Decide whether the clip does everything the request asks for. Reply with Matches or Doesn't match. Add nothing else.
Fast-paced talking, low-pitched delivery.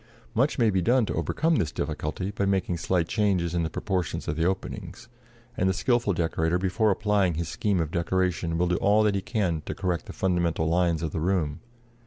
Matches